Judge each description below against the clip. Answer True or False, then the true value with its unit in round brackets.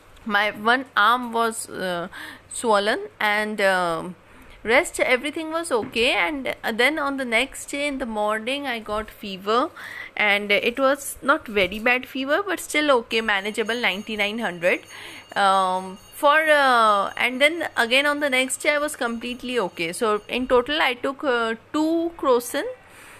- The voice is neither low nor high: False (240 Hz)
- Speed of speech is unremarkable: True (150 wpm)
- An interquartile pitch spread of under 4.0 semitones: False (5.3 semitones)